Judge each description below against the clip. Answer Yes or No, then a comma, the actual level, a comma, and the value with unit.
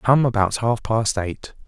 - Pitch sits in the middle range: No, low, 110 Hz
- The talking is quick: No, average, 180 wpm